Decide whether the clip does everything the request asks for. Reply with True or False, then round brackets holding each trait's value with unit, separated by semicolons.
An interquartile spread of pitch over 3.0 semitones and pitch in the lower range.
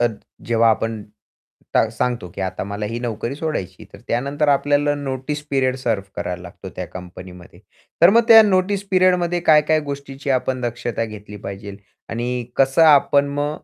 True (5.4 semitones; 130 Hz)